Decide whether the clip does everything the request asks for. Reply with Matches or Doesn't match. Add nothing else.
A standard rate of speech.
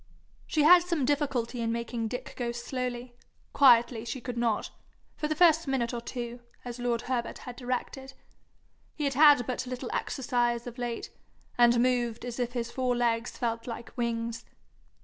Matches